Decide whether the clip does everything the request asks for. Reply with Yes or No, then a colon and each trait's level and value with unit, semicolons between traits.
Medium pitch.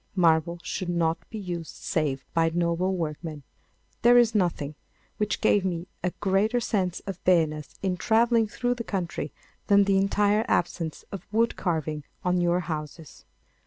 Yes: medium, 180 Hz